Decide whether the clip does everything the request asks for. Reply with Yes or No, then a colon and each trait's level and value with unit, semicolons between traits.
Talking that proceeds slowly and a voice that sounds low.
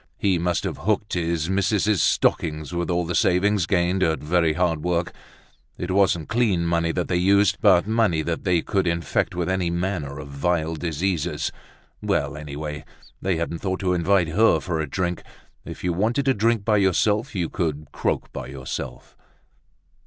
No: average, 175 wpm; very low, 90 Hz